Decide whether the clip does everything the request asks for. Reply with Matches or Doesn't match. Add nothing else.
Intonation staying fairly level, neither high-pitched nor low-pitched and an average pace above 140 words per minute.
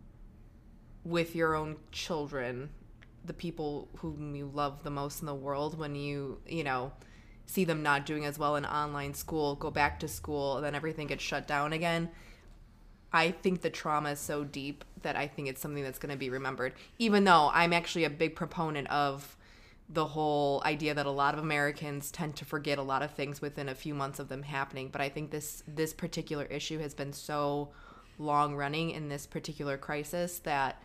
Matches